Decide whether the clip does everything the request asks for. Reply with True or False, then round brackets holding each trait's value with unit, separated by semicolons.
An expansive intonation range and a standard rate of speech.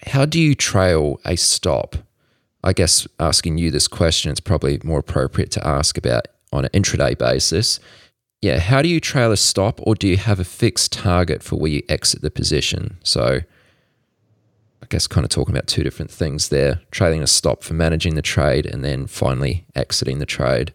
True (6.5 semitones; 195 wpm)